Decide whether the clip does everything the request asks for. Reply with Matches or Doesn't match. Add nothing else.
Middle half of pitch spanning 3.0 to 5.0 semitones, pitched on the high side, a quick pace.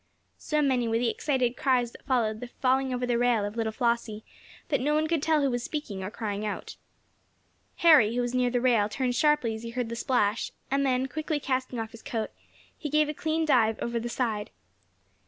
Matches